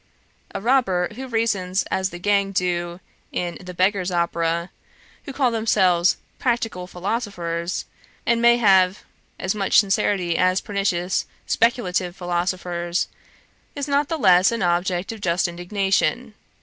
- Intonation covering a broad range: No, average, 3.8 semitones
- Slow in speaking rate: Yes, slow, 130 wpm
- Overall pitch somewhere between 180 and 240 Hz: Yes, medium, 185 Hz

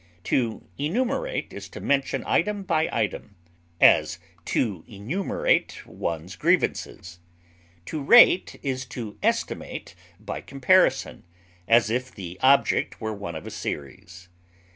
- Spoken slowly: Yes, slow, 120 wpm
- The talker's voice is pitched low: Yes, low, 125 Hz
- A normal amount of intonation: No, wide, 8.8 semitones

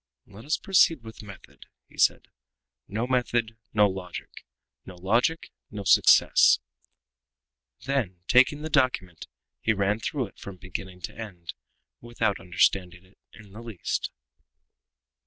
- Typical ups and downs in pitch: Yes, average, 4.1 semitones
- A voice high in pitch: No, low, 105 Hz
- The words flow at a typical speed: No, slow, 130 wpm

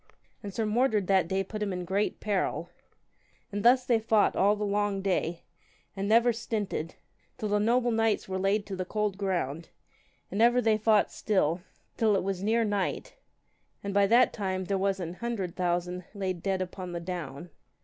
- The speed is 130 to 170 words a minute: No, average, 185 wpm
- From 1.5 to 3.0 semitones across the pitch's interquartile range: Yes, average, 2.7 semitones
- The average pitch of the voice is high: Yes, high, 200 Hz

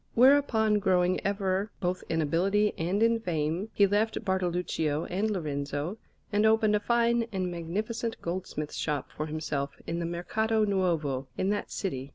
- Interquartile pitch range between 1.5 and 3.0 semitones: No, average, 4.7 semitones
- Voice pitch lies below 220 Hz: Yes, medium, 185 Hz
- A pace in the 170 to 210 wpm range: No, average, 155 wpm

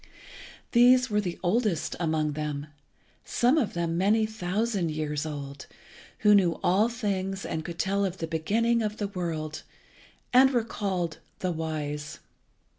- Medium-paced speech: Yes, average, 145 wpm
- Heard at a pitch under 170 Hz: No, medium, 185 Hz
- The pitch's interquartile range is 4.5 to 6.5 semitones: Yes, wide, 5.4 semitones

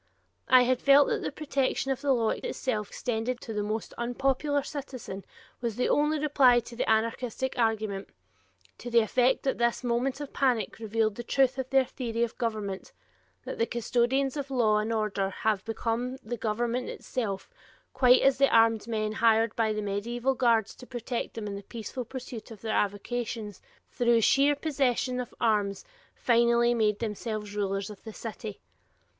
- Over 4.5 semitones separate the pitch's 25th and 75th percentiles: No, average, 2.9 semitones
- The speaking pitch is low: No, high, 235 Hz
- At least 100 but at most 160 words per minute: No, average, 175 wpm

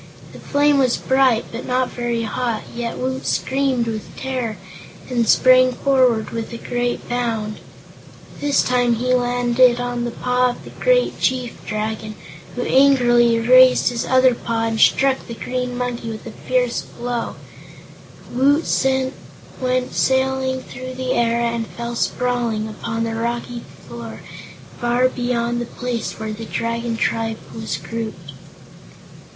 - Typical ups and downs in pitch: No, narrow, 1.8 semitones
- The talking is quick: No, average, 145 wpm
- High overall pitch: Yes, high, 240 Hz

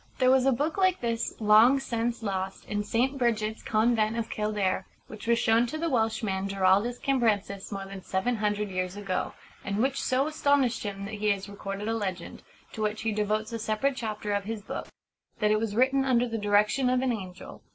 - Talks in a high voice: Yes, high, 220 Hz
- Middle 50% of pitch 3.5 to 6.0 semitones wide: No, average, 3.1 semitones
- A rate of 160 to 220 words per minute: Yes, fast, 205 wpm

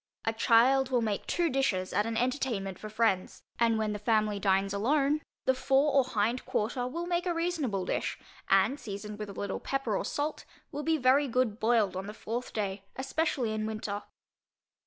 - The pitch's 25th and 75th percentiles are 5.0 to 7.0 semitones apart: No, average, 4.6 semitones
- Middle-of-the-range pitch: No, high, 230 Hz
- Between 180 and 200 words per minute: Yes, average, 190 wpm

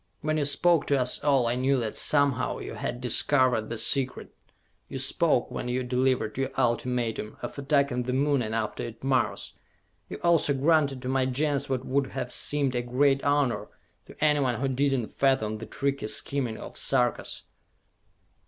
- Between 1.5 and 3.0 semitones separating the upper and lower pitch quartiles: Yes, narrow, 2.4 semitones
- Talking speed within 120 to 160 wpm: No, average, 180 wpm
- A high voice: No, low, 130 Hz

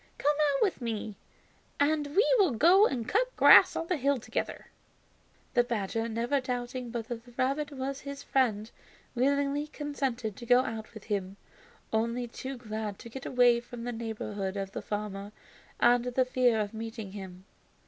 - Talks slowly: No, average, 170 wpm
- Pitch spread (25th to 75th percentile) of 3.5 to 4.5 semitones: Yes, average, 3.8 semitones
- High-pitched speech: Yes, high, 240 Hz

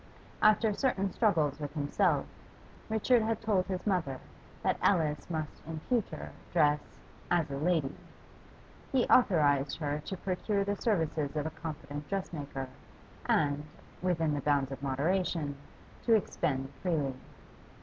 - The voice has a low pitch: No, medium, 160 Hz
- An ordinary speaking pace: No, slow, 130 wpm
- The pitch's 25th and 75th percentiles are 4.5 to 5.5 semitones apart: Yes, average, 5.1 semitones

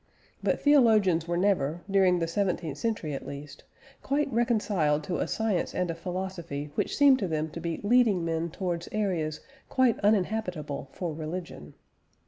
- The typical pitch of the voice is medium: Yes, medium, 180 Hz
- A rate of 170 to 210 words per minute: No, average, 155 wpm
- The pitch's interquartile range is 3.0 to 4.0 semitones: No, average, 4.8 semitones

